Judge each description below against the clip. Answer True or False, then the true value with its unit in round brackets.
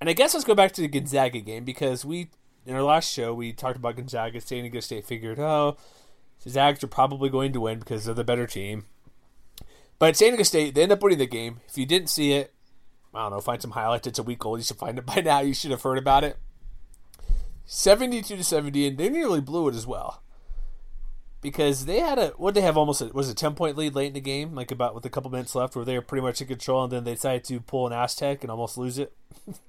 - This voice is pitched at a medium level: False (130 Hz)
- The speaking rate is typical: False (260 wpm)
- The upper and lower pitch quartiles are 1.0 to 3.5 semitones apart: True (3.1 semitones)